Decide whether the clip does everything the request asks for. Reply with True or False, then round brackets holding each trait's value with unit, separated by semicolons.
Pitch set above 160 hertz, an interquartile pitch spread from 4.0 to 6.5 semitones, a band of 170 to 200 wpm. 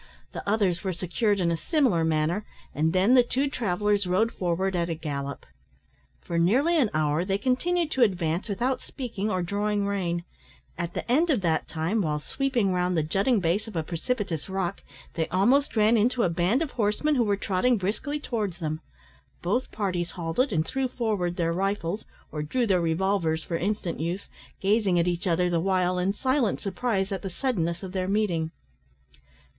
True (190 Hz; 4.7 semitones; 185 wpm)